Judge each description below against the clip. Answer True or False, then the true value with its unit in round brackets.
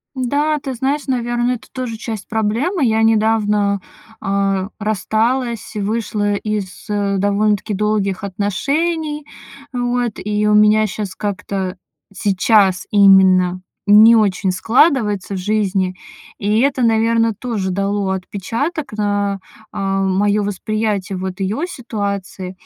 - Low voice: False (210 Hz)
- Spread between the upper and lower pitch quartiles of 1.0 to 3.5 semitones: True (2.8 semitones)